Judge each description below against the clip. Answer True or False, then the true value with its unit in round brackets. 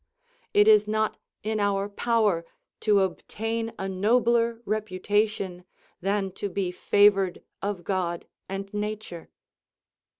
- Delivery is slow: True (110 wpm)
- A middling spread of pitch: False (2.1 semitones)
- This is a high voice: True (205 Hz)